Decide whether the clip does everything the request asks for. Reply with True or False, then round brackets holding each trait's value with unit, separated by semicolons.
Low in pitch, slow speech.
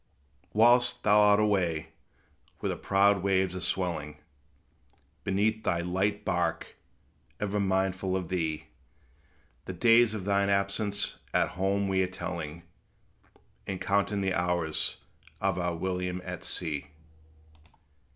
True (95 Hz; 120 wpm)